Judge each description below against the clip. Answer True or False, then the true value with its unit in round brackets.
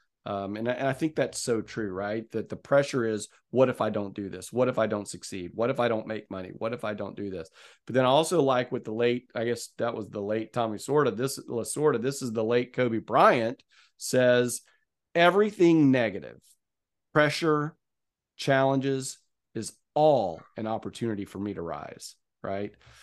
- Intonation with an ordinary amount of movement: True (4.0 semitones)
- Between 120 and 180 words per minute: False (195 wpm)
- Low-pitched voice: True (115 Hz)